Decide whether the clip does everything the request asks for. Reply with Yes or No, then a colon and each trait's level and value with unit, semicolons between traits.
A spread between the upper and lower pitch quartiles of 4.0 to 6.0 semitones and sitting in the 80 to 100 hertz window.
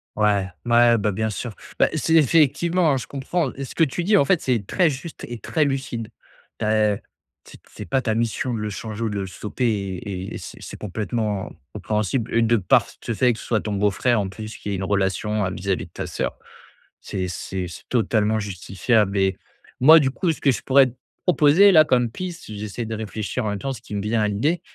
No: average, 4.5 semitones; low, 110 Hz